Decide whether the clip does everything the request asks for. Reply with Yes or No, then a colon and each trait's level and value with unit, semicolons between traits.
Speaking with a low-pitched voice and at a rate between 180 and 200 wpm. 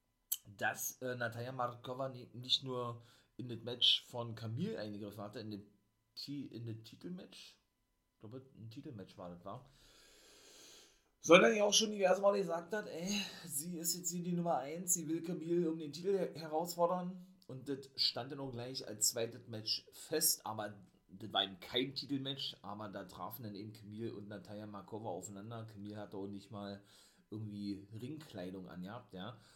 No: low, 120 Hz; average, 165 wpm